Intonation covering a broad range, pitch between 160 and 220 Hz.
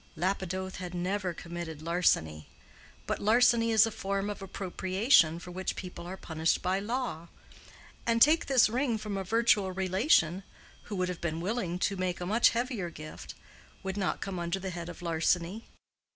No: average, 3.4 semitones; high, 190 Hz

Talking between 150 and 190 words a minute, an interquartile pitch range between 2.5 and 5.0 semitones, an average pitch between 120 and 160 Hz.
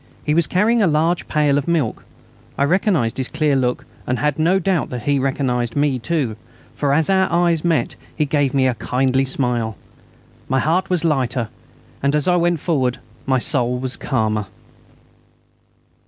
Yes: average, 170 wpm; average, 4.7 semitones; medium, 140 Hz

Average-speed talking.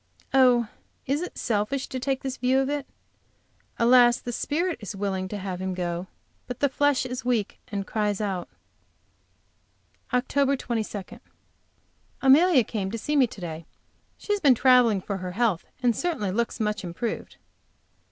Yes: average, 160 wpm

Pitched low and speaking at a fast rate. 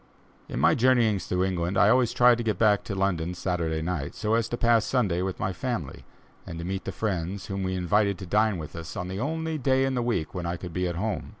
Yes: very low, 95 Hz; fast, 255 wpm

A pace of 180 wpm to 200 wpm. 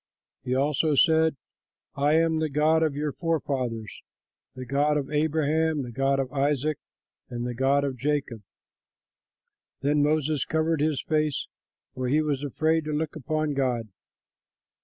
No: average, 145 wpm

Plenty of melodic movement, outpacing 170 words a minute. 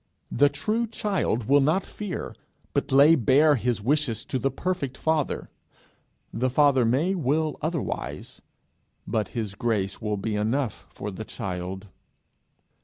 No: wide, 5.9 semitones; slow, 135 wpm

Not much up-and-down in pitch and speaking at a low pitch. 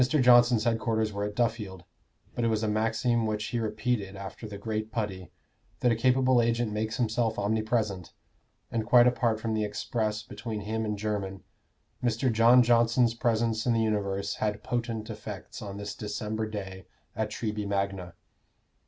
Yes: narrow, 2.0 semitones; low, 110 Hz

